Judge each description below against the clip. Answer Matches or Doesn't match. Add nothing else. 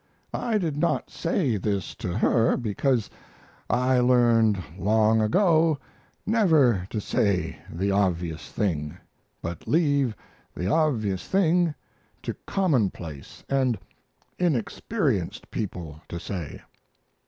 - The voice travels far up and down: Matches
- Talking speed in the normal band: Doesn't match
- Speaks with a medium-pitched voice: Doesn't match